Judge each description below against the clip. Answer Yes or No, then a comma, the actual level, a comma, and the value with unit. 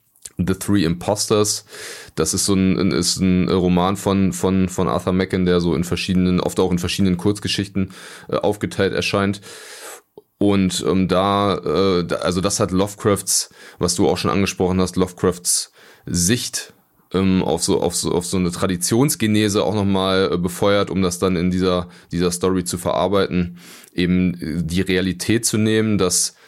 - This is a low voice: Yes, very low, 95 Hz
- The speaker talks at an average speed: Yes, average, 165 wpm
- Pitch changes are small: Yes, narrow, 1.7 semitones